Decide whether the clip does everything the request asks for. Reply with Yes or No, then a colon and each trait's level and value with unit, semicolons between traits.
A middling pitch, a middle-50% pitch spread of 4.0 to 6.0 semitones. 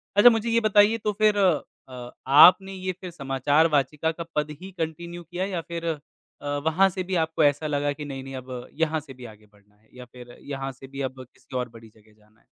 Yes: medium, 150 Hz; wide, 5.5 semitones